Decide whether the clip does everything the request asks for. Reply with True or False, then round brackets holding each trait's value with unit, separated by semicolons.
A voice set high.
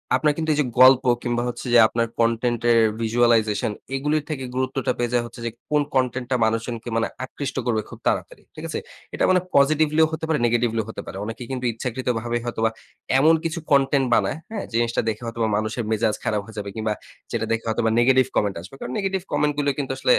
False (120 Hz)